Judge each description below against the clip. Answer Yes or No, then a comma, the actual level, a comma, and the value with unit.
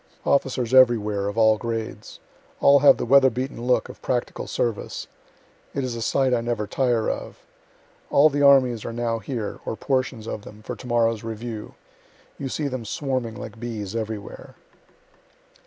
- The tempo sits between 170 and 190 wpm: No, average, 160 wpm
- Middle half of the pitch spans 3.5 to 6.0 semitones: No, average, 2.8 semitones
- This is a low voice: Yes, low, 120 Hz